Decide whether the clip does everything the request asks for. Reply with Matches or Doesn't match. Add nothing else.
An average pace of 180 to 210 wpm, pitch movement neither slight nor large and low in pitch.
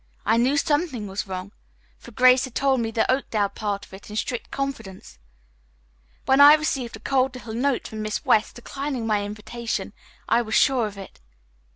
Doesn't match